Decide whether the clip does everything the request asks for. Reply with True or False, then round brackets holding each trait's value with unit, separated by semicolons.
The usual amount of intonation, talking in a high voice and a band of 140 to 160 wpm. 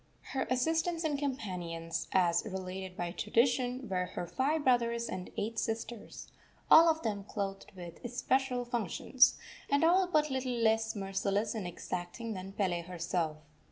False (5.9 semitones; 225 Hz; 145 wpm)